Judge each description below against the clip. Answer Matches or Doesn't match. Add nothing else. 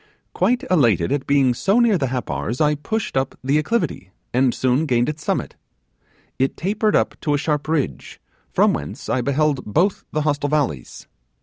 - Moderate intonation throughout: Matches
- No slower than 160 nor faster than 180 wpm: Matches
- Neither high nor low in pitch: Matches